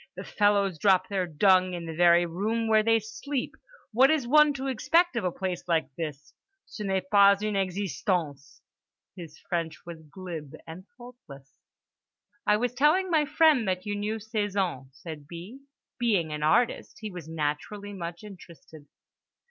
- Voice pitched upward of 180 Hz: Yes, high, 190 Hz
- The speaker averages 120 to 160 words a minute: Yes, average, 155 wpm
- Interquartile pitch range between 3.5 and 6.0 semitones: Yes, average, 4.8 semitones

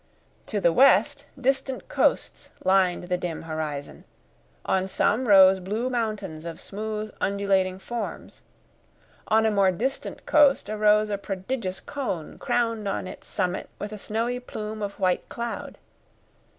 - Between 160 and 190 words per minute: No, slow, 135 wpm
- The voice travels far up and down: No, average, 3.8 semitones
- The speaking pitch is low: No, high, 210 Hz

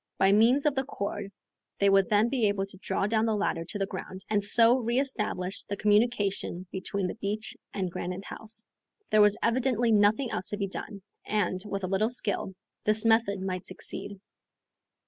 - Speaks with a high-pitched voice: Yes, high, 205 Hz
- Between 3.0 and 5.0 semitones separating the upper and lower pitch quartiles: No, narrow, 2.5 semitones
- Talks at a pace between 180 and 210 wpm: Yes, average, 185 wpm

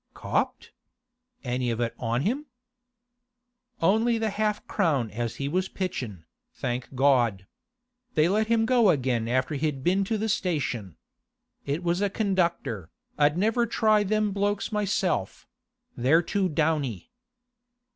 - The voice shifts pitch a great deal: Yes, wide, 8.4 semitones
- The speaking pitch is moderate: Yes, medium, 165 Hz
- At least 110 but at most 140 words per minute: Yes, slow, 135 wpm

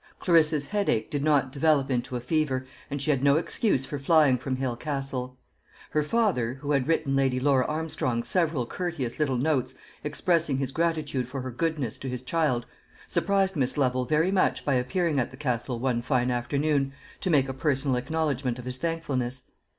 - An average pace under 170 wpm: No, average, 180 wpm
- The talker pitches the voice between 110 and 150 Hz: Yes, low, 135 Hz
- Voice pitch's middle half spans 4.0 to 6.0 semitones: No, average, 3.4 semitones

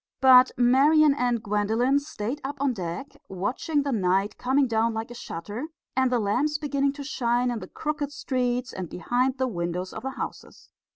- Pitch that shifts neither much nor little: Yes, average, 4.4 semitones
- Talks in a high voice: Yes, very high, 250 Hz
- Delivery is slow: No, average, 180 wpm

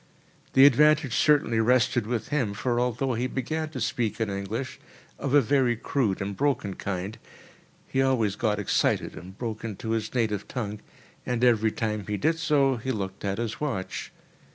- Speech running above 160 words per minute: Yes, average, 170 wpm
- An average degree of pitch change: Yes, average, 4.1 semitones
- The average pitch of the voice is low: Yes, low, 115 Hz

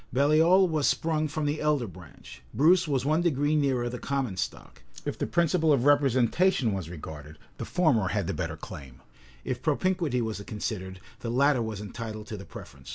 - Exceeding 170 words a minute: Yes, average, 180 wpm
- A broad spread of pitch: Yes, wide, 6.4 semitones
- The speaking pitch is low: Yes, low, 130 Hz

